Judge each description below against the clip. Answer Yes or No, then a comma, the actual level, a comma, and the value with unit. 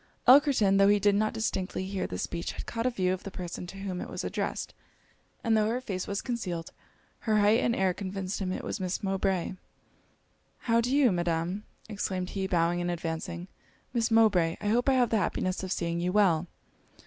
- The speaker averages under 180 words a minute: No, fast, 205 wpm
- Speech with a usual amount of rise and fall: Yes, average, 3.5 semitones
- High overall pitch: Yes, high, 195 Hz